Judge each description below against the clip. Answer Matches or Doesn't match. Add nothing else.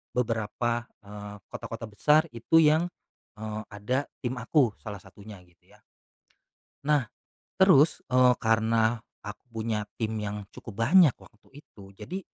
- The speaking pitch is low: Matches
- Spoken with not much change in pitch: Doesn't match